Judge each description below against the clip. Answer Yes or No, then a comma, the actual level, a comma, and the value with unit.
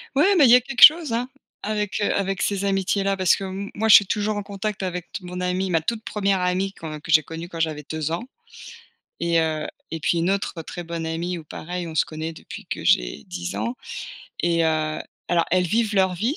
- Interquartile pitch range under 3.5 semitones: No, average, 3.8 semitones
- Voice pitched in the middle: Yes, medium, 180 Hz